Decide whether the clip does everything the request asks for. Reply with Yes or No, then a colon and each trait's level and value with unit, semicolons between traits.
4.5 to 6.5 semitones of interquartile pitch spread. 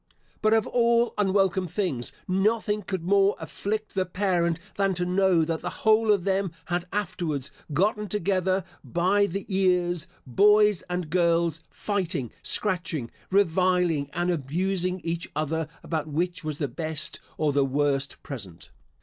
No: average, 3.7 semitones